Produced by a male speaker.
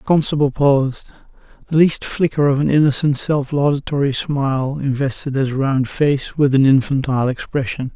Yes: male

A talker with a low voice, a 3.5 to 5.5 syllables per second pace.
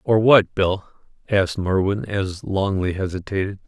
Yes: low, 100 Hz; 4.5 syllables/s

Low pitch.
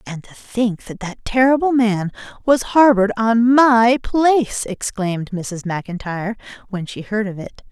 No: high, 220 Hz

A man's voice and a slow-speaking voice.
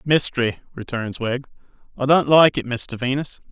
No: male; average, 155 wpm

